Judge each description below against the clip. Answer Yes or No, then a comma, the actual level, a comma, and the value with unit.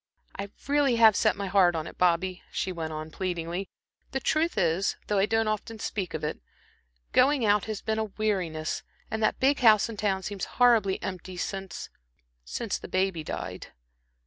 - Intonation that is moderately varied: Yes, average, 3.8 semitones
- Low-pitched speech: No, high, 195 Hz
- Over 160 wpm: Yes, average, 180 wpm